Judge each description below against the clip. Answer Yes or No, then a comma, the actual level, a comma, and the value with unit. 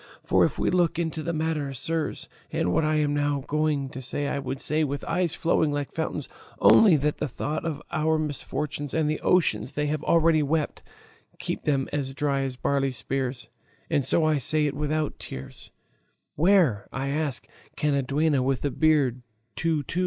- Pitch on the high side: No, medium, 150 Hz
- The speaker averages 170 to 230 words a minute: Yes, average, 190 wpm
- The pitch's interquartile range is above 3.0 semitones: No, narrow, 2.4 semitones